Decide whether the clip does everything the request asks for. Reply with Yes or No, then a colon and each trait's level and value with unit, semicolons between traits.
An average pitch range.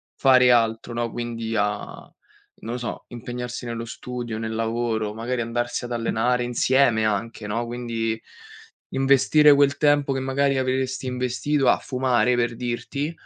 No: narrow, 2.3 semitones